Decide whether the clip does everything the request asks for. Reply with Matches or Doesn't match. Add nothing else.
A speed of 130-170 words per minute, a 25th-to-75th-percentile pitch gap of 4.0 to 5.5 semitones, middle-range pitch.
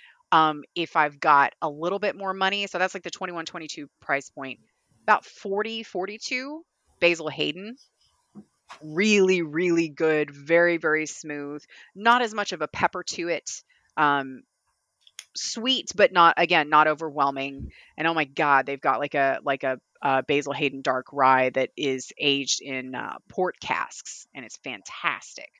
Matches